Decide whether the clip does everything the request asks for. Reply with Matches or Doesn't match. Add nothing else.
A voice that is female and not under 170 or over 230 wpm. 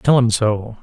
Doesn't match